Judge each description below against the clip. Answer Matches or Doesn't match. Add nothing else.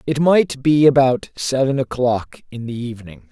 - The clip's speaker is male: Matches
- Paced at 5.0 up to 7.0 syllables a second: Doesn't match